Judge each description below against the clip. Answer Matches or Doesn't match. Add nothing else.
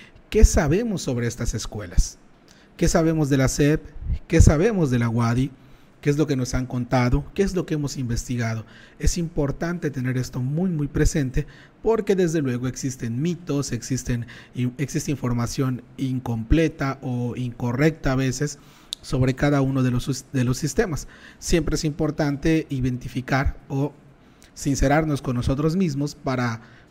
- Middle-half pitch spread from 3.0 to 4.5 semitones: Matches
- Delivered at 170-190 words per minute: Doesn't match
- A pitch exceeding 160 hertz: Doesn't match